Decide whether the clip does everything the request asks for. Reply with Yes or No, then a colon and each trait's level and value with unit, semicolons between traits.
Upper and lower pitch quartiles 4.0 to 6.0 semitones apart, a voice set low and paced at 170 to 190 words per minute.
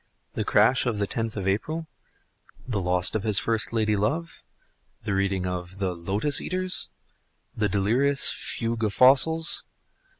No: average, 5.2 semitones; low, 110 Hz; average, 145 wpm